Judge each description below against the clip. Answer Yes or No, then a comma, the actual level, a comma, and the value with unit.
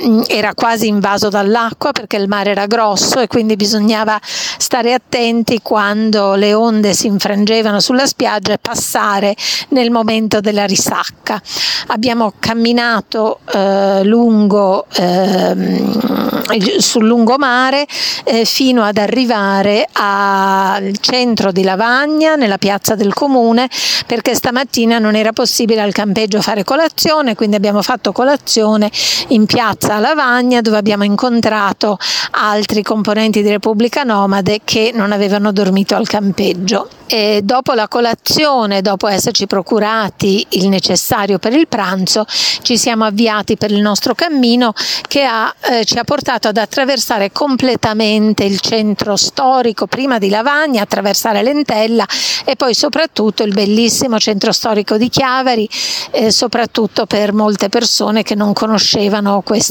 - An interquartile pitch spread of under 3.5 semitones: Yes, average, 2.7 semitones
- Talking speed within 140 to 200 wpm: No, average, 130 wpm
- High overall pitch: Yes, high, 220 Hz